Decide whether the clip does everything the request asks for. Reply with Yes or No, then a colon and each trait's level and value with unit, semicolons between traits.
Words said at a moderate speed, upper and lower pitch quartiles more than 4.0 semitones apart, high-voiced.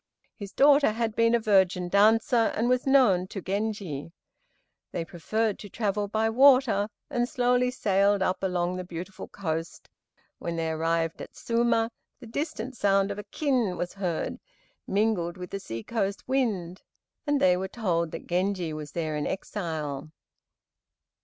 Yes: average, 155 wpm; average, 4.5 semitones; high, 200 Hz